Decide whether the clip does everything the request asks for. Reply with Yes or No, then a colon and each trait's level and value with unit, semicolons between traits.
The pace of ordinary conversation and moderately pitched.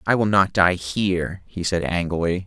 No: average, 195 wpm; very low, 90 Hz